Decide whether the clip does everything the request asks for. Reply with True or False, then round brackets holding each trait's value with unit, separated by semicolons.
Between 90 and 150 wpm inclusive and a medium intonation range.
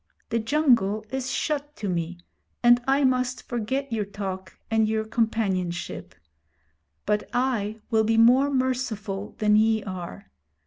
True (135 wpm; 3.7 semitones)